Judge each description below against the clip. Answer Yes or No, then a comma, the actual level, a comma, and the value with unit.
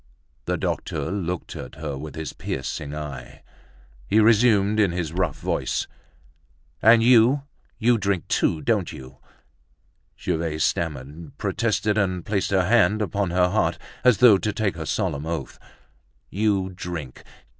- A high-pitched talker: No, very low, 95 Hz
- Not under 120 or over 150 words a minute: Yes, average, 140 wpm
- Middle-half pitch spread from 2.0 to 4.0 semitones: No, average, 5.2 semitones